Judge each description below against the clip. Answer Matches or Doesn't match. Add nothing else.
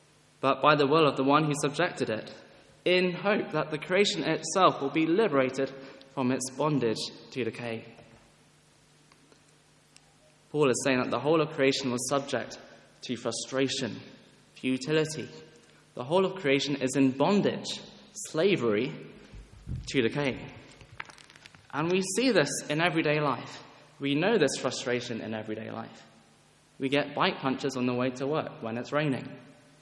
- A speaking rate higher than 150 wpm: Doesn't match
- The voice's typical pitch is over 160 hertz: Doesn't match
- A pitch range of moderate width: Matches